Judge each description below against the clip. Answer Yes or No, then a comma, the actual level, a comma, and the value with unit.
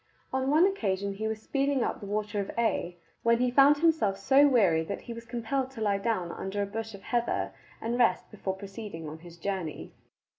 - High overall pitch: Yes, high, 220 Hz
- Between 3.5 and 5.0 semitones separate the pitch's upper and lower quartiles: Yes, average, 4.2 semitones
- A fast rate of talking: Yes, fast, 210 wpm